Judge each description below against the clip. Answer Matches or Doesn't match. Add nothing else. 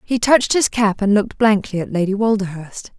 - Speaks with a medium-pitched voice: Doesn't match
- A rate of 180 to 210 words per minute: Matches